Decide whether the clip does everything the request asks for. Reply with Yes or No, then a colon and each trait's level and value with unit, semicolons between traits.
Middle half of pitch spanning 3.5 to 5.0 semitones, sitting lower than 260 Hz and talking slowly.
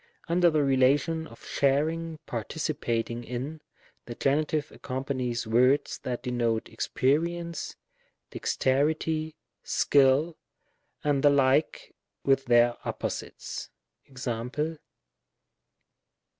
Yes: average, 3.9 semitones; low, 135 Hz; slow, 85 wpm